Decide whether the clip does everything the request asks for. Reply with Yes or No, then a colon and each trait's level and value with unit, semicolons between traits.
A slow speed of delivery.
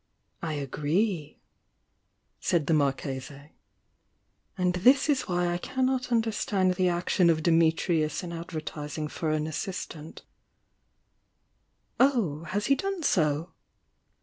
Yes: slow, 120 wpm